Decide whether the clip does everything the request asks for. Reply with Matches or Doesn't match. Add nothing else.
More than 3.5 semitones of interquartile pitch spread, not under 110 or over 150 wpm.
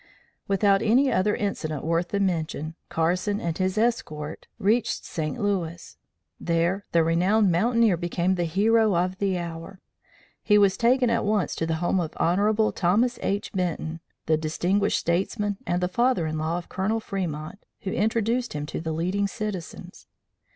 Doesn't match